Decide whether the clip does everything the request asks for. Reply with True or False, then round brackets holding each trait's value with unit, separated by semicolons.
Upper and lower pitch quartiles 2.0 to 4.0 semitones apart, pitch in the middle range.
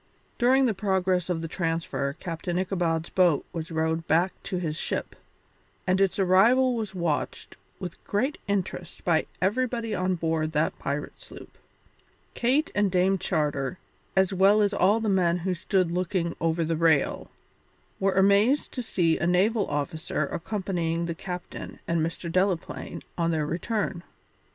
True (3.1 semitones; 180 Hz)